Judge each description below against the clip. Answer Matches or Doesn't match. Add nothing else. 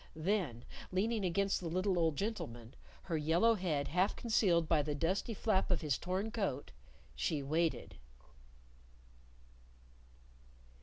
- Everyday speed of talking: Doesn't match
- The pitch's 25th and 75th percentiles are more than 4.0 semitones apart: Matches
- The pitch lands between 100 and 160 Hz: Doesn't match